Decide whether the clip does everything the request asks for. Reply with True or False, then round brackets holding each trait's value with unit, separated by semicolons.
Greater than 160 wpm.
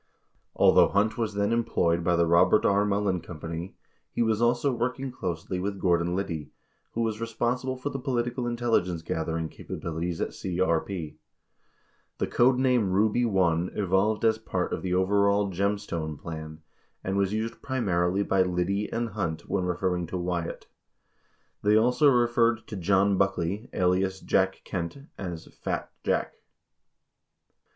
False (155 wpm)